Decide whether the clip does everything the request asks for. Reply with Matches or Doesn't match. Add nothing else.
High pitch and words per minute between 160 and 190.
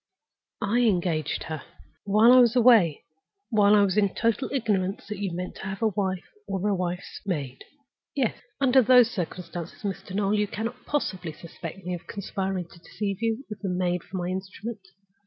Matches